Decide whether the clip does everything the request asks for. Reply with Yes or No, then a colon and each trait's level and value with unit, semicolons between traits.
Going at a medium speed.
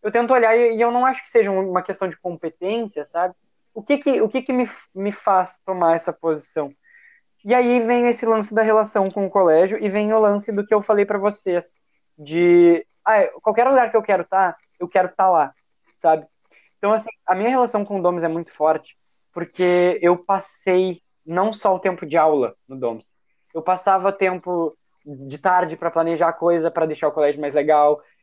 No: fast, 210 wpm